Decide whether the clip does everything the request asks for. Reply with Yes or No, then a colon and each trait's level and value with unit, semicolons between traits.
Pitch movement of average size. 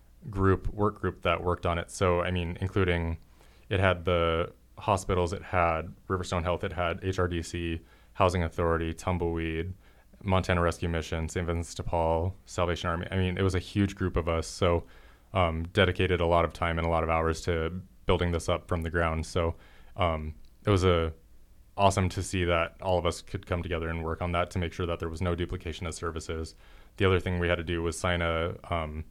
No: narrow, 1.9 semitones